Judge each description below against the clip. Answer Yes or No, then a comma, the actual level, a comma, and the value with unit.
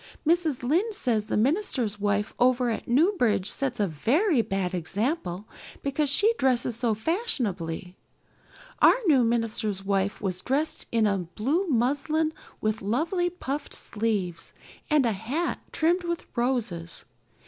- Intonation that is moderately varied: No, wide, 6.9 semitones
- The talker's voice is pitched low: No, high, 240 Hz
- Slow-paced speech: Yes, slow, 130 wpm